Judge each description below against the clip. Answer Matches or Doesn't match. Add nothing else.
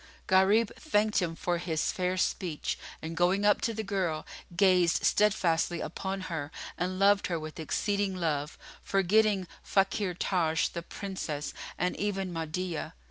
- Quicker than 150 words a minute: Doesn't match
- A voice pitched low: Doesn't match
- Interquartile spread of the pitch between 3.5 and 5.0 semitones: Doesn't match